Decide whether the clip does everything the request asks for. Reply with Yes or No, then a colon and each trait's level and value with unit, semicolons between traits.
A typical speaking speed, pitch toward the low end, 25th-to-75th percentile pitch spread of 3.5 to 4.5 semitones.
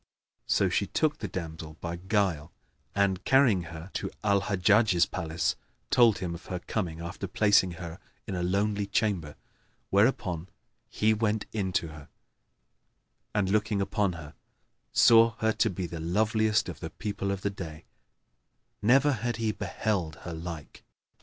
Yes: average, 155 wpm; low, 100 Hz; average, 3.9 semitones